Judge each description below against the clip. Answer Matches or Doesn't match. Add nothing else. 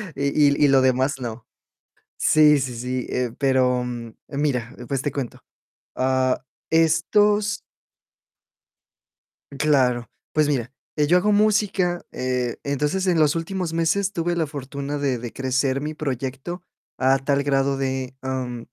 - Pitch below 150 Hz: Matches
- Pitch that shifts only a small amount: Doesn't match